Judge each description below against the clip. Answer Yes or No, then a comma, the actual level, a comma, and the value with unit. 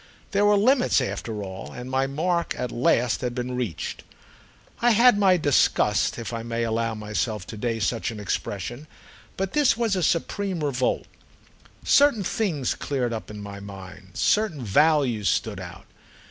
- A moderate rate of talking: Yes, average, 165 wpm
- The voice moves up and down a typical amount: No, wide, 8.6 semitones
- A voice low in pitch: Yes, low, 125 Hz